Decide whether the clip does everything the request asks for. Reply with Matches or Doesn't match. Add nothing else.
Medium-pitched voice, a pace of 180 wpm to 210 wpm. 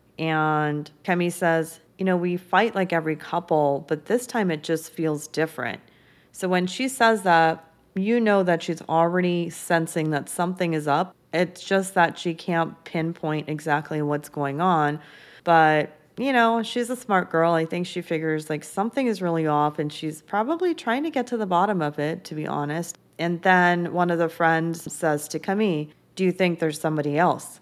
Matches